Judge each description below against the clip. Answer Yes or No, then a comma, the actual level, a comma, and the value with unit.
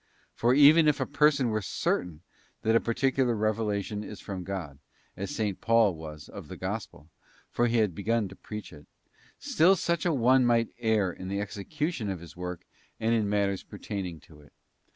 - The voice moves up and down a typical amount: Yes, average, 4.3 semitones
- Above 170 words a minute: Yes, average, 185 wpm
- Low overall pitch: Yes, low, 105 Hz